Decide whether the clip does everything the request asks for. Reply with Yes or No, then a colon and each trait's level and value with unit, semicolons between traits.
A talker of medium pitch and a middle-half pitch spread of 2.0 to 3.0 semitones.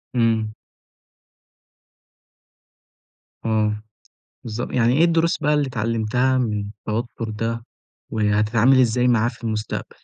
No: low, 115 Hz; narrow, 2.4 semitones